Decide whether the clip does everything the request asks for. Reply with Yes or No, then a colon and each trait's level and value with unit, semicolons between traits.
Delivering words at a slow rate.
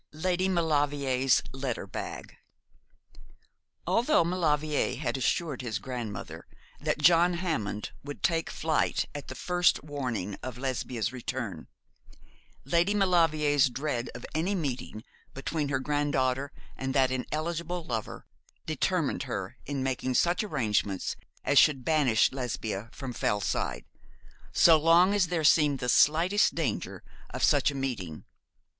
Yes: slow, 125 wpm